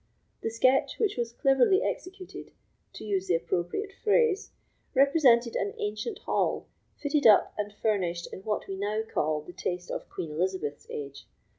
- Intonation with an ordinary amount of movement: No, wide, 7.4 semitones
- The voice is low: No, high, 215 Hz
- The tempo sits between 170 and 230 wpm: No, average, 155 wpm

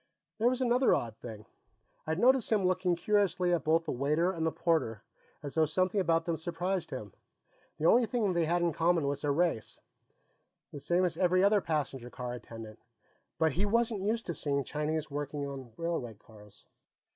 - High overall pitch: No, medium, 165 Hz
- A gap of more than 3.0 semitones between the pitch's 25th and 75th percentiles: Yes, average, 4.7 semitones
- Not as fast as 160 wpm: No, average, 185 wpm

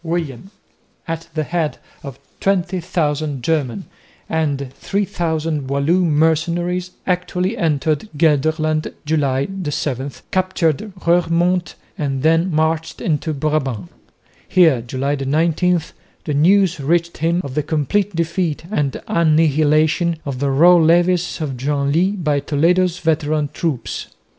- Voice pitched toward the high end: No, medium, 160 Hz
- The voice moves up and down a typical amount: Yes, average, 3.1 semitones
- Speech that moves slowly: Yes, slow, 115 wpm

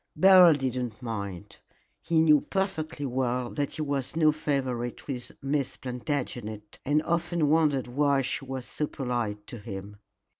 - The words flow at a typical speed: Yes, average, 150 wpm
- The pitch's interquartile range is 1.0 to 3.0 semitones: No, average, 4.0 semitones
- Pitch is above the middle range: No, low, 135 Hz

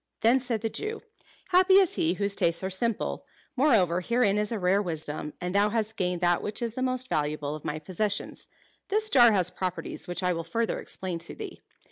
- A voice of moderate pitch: No, high, 200 Hz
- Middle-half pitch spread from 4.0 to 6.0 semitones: Yes, average, 5.2 semitones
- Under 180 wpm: No, fast, 205 wpm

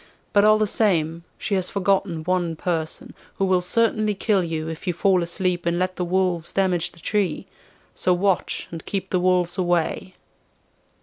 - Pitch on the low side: No, medium, 180 Hz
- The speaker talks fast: No, average, 175 wpm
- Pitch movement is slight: Yes, narrow, 2.2 semitones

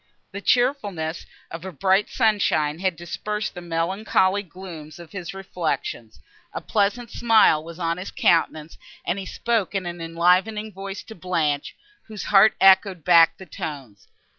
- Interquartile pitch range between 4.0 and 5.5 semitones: No, average, 3.5 semitones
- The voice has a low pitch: No, medium, 185 Hz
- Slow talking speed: No, average, 150 wpm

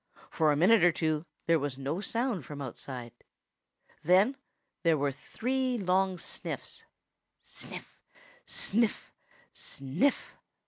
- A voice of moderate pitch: Yes, medium, 170 Hz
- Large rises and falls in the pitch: Yes, wide, 6.8 semitones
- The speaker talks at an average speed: No, slow, 110 wpm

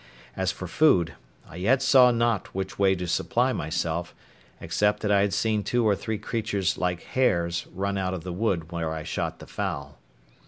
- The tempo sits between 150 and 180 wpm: No, average, 190 wpm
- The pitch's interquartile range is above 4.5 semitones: No, average, 4.1 semitones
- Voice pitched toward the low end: Yes, very low, 95 Hz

